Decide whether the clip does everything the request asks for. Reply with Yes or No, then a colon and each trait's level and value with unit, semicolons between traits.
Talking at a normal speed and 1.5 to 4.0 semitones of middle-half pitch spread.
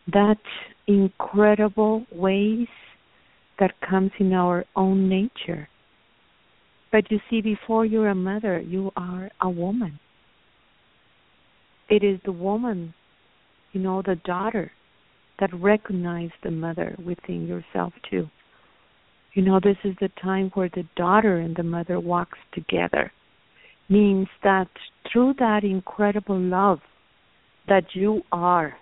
No: slow, 125 wpm; narrow, 2.5 semitones